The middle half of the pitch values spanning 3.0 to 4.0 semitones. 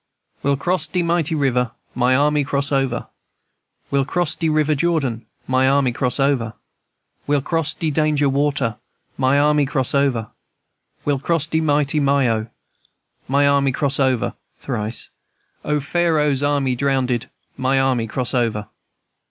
No: narrow, 2.5 semitones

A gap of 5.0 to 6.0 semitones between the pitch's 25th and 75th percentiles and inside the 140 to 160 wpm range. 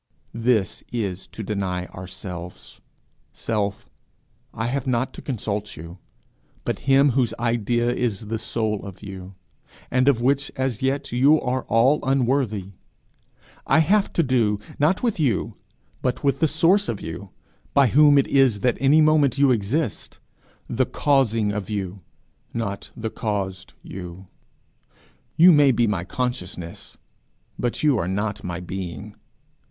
Yes: wide, 5.4 semitones; average, 145 wpm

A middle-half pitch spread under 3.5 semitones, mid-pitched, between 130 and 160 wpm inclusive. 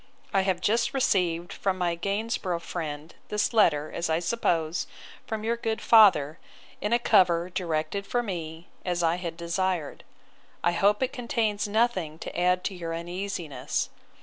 No: average, 3.8 semitones; medium, 180 Hz; average, 155 wpm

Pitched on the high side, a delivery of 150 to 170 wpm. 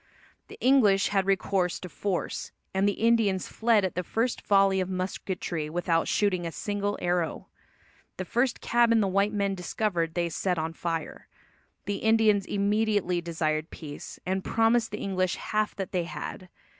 Yes: high, 195 Hz; average, 160 wpm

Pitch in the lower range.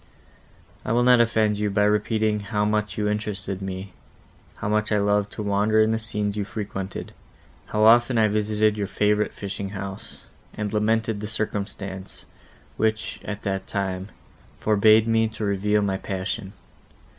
Yes: low, 105 Hz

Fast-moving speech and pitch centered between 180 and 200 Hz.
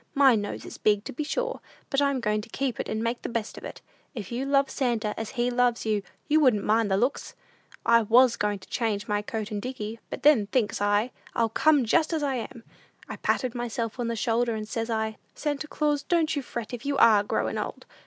No: fast, 235 wpm; high, 235 Hz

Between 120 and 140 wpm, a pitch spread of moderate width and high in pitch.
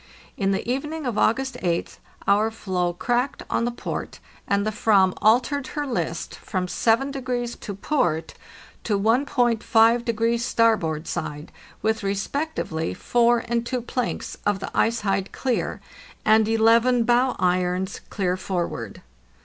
Yes: slow, 135 wpm; average, 3.9 semitones; high, 225 Hz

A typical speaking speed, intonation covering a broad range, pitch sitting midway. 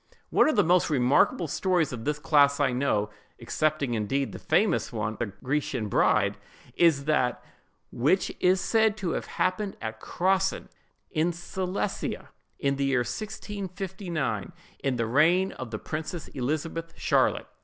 Yes: average, 145 wpm; wide, 6.2 semitones; medium, 155 Hz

